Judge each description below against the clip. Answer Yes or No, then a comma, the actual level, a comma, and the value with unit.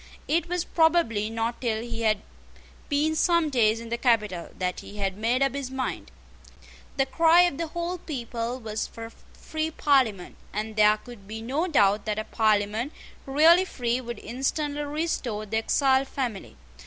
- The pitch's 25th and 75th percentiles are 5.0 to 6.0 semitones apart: Yes, wide, 5.5 semitones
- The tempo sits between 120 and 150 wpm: No, average, 170 wpm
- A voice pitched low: No, high, 240 Hz